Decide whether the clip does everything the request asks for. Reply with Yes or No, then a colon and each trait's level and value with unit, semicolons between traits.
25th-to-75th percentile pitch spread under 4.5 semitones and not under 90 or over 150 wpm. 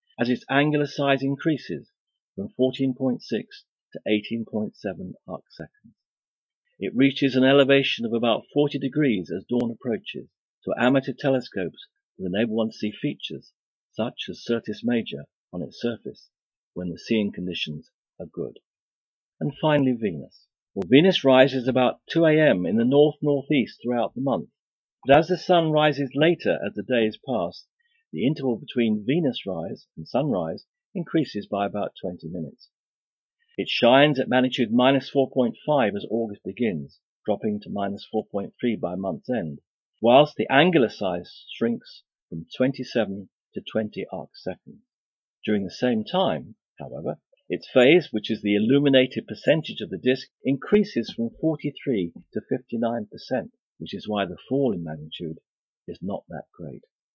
No: average, 5.2 semitones; average, 145 wpm